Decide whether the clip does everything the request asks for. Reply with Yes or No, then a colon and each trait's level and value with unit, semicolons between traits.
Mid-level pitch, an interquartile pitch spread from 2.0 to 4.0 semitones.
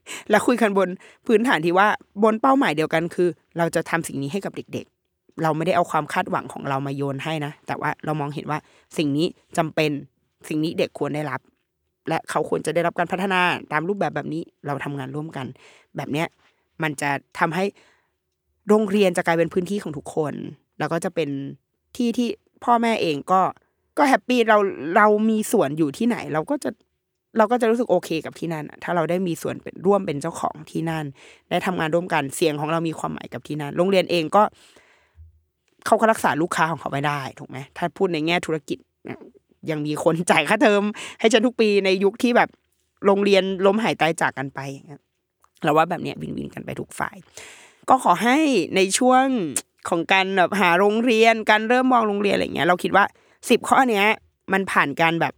No: medium, 175 Hz; average, 5.2 semitones